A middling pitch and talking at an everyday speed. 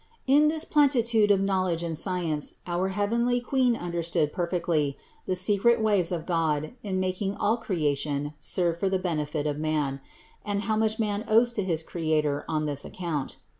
Yes: medium, 180 Hz; average, 170 wpm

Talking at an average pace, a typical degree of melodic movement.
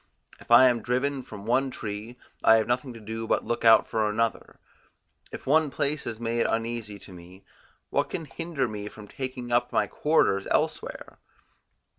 Yes: average, 175 wpm; average, 3.1 semitones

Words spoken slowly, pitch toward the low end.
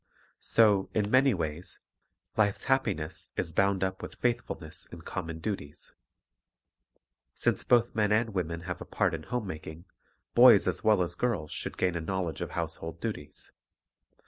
No: average, 160 wpm; very low, 95 Hz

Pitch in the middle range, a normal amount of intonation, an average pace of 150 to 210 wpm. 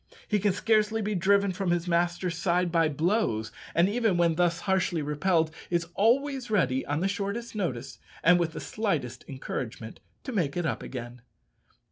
Yes: medium, 175 Hz; average, 4.3 semitones; average, 170 wpm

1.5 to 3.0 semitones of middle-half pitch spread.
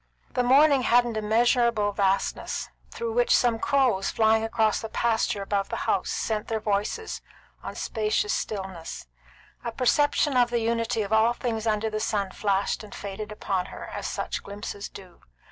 Yes: average, 2.7 semitones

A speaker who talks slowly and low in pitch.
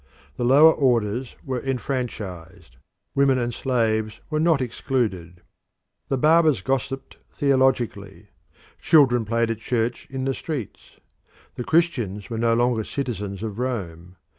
Yes: slow, 125 wpm; low, 120 Hz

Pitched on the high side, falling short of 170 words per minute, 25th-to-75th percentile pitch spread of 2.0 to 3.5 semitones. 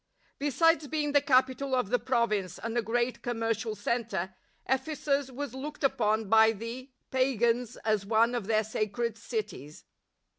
Yes: high, 240 Hz; average, 150 wpm; average, 3.2 semitones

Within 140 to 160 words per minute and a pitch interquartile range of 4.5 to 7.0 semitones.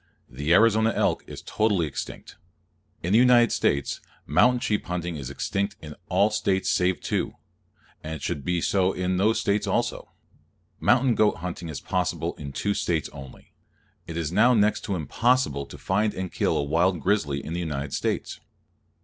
No: average, 170 wpm; wide, 5.4 semitones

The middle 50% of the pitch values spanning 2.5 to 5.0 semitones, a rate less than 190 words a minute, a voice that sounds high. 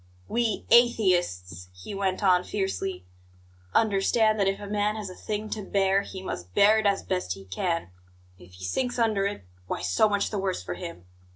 No: average, 3.5 semitones; average, 195 wpm; high, 195 Hz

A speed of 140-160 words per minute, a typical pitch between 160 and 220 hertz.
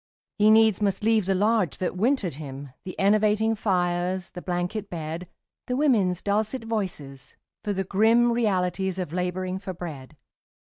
Yes: average, 150 wpm; high, 190 Hz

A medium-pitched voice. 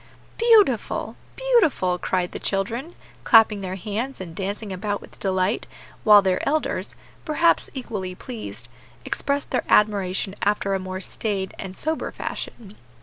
No: high, 205 Hz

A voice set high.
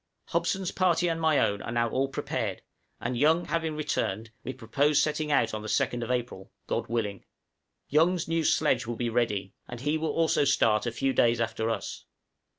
No: low, 130 Hz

